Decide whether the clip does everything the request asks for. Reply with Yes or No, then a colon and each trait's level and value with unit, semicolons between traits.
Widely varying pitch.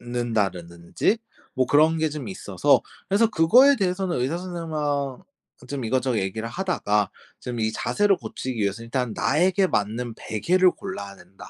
Yes: wide, 8.4 semitones